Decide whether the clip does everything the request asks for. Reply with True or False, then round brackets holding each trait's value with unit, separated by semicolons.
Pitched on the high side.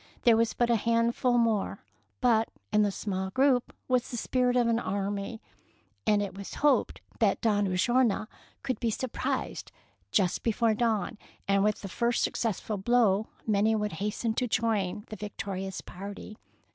True (220 Hz)